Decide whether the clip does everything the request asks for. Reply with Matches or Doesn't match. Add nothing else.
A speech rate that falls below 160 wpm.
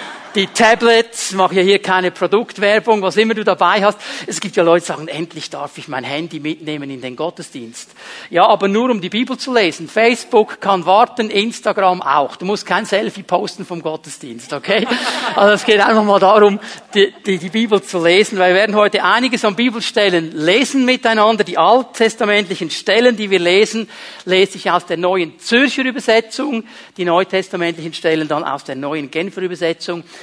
Doesn't match